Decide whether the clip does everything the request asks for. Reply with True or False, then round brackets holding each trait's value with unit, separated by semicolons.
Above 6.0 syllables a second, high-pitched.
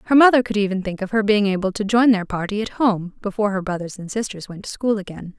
True (6.4 syllables/s; 205 Hz)